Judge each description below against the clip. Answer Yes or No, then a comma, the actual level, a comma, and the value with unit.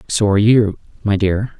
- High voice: No, low, 105 Hz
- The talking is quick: No, average, 190 wpm